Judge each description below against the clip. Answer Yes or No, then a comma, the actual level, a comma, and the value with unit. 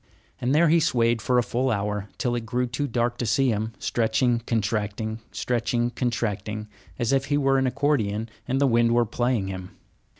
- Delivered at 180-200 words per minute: Yes, average, 190 wpm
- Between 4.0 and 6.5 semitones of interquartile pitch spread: No, average, 2.8 semitones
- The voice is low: Yes, low, 120 Hz